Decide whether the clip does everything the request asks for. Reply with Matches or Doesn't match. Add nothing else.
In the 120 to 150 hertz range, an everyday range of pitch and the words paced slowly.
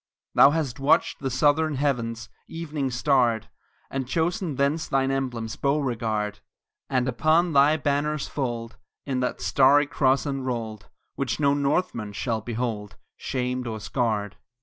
Matches